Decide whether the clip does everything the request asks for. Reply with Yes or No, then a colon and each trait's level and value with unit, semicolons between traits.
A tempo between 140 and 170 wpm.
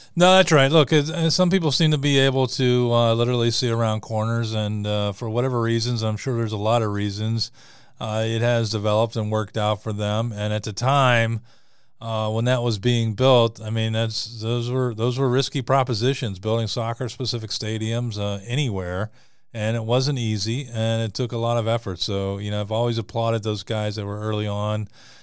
No: average, 195 wpm